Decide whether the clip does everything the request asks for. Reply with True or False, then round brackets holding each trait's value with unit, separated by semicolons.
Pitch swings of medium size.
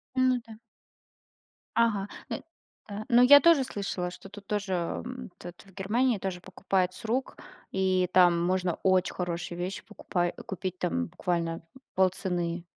True (3.7 semitones)